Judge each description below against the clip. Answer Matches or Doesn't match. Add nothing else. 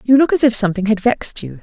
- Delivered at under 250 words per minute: Doesn't match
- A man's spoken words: Doesn't match